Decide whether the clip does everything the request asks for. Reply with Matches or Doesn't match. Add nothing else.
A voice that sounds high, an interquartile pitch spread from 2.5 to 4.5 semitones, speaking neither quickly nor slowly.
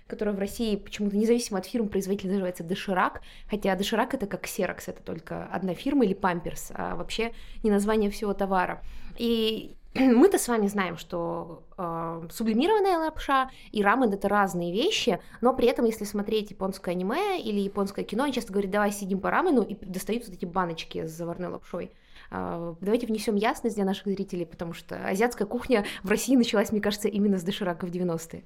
Doesn't match